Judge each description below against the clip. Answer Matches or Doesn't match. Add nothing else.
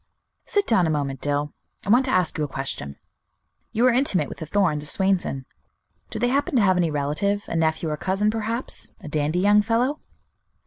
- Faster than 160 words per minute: Matches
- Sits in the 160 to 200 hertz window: Matches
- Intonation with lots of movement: Matches